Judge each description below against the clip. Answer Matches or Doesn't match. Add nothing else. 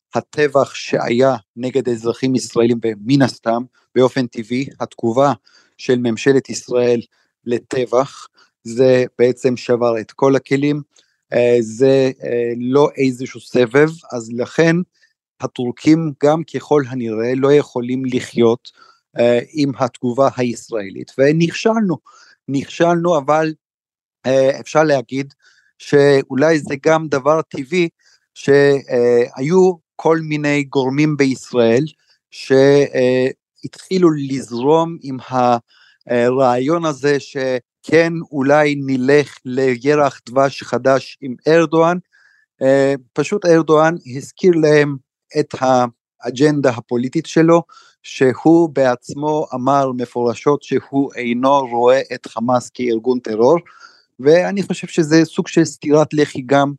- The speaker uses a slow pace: Matches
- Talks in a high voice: Doesn't match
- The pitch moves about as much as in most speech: Matches